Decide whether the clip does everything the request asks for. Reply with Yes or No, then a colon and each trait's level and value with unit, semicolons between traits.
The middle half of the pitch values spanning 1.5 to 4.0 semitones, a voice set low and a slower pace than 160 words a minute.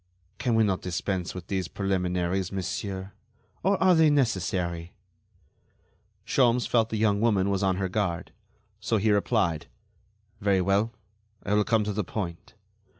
Yes: average, 3.2 semitones; low, 100 Hz; average, 150 wpm